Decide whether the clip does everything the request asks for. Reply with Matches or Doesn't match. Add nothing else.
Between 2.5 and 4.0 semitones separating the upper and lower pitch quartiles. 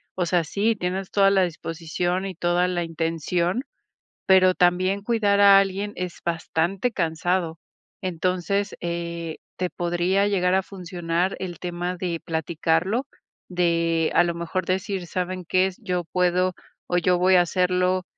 Doesn't match